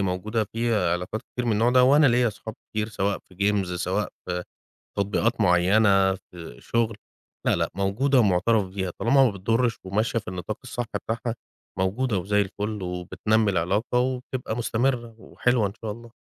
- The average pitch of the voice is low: Yes, low, 110 Hz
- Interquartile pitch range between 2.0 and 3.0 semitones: No, average, 3.5 semitones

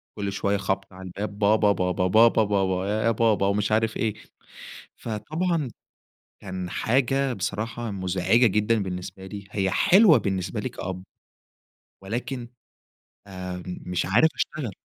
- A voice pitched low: Yes, low, 100 Hz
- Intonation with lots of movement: No, average, 3.5 semitones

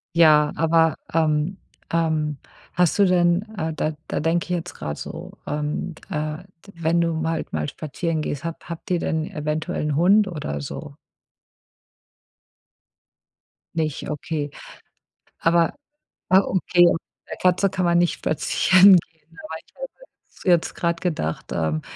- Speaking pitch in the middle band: Yes, medium, 165 Hz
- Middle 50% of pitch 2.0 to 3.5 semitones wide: Yes, narrow, 2.4 semitones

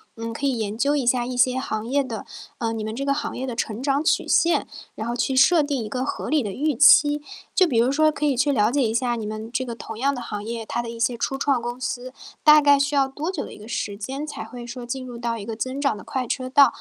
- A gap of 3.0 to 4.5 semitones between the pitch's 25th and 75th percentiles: Yes, average, 3.3 semitones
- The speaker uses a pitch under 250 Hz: No, very high, 255 Hz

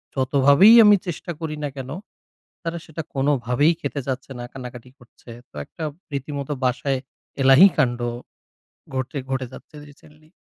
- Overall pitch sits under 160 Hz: Yes, medium, 140 Hz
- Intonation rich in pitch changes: No, average, 2.8 semitones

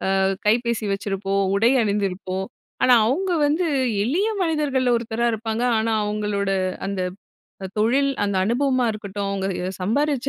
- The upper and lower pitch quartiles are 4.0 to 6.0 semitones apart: Yes, average, 4.5 semitones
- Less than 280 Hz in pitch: Yes, high, 220 Hz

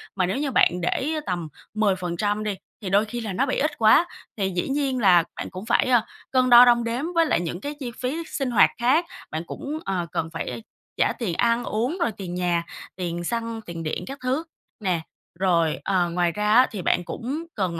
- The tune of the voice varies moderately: No, wide, 6.0 semitones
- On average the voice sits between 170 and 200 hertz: No, high, 215 Hz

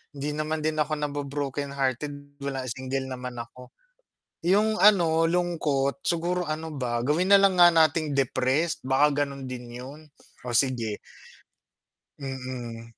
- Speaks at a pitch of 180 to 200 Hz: No, medium, 140 Hz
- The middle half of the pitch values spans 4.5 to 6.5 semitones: No, average, 3.5 semitones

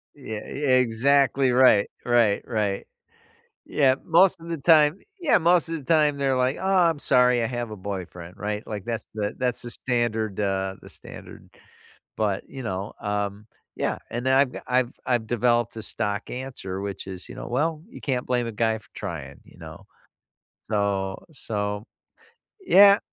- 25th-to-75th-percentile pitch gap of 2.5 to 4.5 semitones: No, average, 4.9 semitones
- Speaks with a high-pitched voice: No, low, 120 Hz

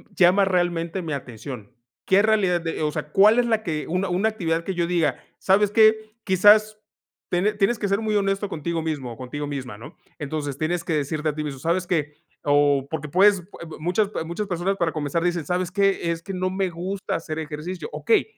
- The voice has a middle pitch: Yes, medium, 175 Hz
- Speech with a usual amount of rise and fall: Yes, average, 4.3 semitones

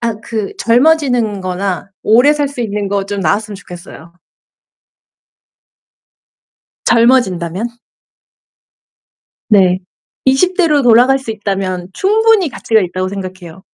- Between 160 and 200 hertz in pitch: No, high, 215 Hz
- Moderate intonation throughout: No, wide, 5.8 semitones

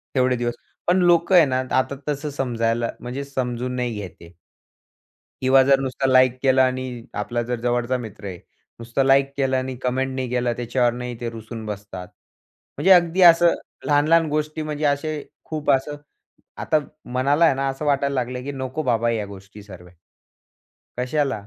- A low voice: Yes, low, 130 Hz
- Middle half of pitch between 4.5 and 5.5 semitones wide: No, average, 3.0 semitones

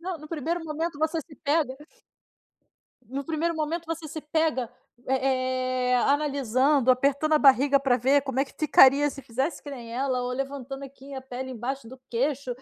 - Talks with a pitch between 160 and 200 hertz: No, very high, 275 Hz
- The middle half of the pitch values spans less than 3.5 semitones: Yes, average, 2.9 semitones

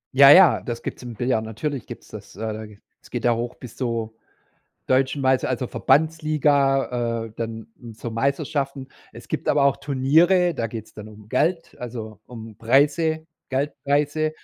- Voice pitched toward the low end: Yes, low, 130 Hz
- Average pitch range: Yes, average, 4.0 semitones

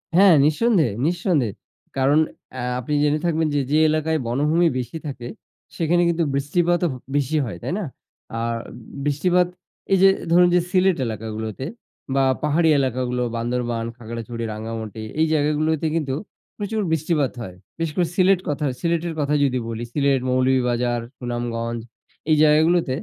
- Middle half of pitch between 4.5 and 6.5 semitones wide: Yes, wide, 5.5 semitones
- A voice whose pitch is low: No, medium, 145 Hz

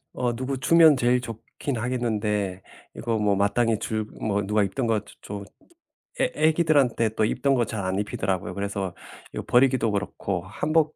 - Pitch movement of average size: Yes, average, 4.1 semitones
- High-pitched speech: No, low, 115 Hz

